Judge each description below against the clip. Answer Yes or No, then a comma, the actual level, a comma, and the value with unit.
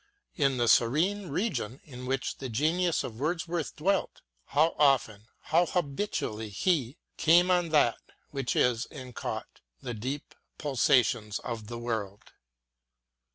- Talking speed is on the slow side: Yes, slow, 130 wpm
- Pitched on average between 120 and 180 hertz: Yes, low, 135 Hz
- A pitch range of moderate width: No, wide, 5.7 semitones